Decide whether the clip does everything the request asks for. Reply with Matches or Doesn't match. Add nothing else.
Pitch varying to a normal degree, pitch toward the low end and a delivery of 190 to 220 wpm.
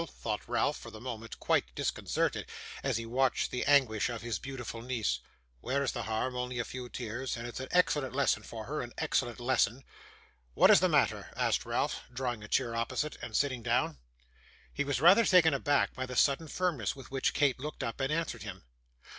Matches